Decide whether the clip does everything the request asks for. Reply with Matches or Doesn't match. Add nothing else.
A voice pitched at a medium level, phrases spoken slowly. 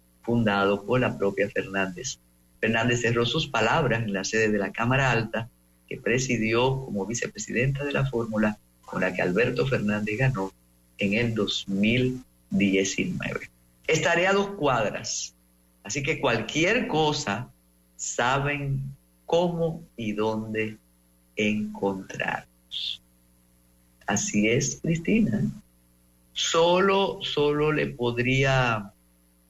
Doesn't match